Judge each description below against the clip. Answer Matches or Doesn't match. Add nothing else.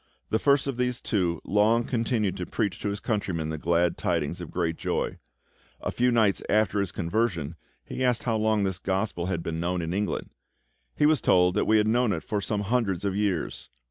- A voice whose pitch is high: Doesn't match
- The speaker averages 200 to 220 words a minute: Matches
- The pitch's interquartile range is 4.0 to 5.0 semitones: Matches